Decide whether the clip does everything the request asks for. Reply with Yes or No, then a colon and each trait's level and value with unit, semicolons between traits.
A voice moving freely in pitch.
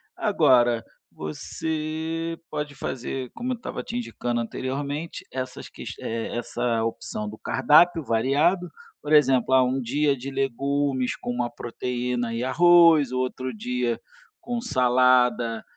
No: average, 3.8 semitones